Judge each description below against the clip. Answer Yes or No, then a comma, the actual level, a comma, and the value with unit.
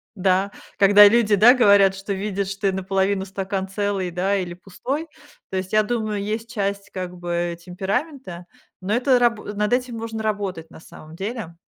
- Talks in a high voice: Yes, high, 200 Hz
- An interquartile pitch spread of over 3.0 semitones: No, narrow, 2.4 semitones